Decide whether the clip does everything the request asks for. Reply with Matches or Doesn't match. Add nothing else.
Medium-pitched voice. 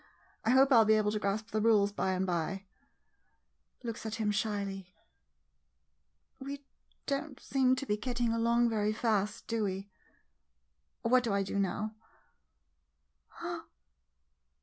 Doesn't match